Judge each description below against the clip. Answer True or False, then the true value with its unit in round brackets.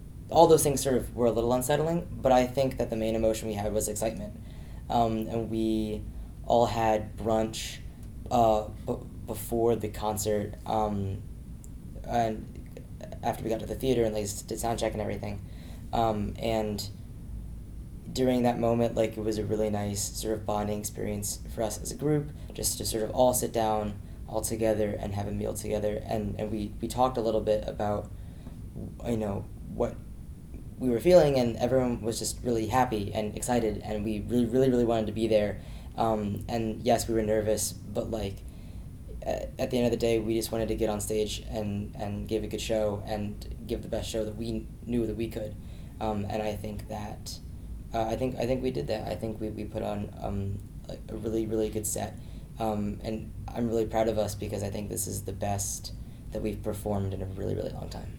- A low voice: True (110 Hz)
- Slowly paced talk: False (205 wpm)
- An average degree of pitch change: False (1.8 semitones)